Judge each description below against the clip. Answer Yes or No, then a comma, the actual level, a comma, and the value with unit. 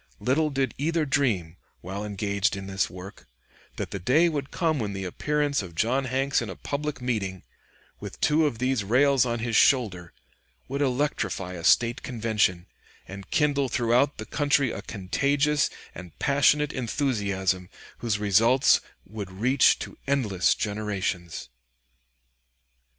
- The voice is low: Yes, low, 120 Hz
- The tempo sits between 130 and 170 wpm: Yes, average, 140 wpm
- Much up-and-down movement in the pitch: Yes, wide, 6.2 semitones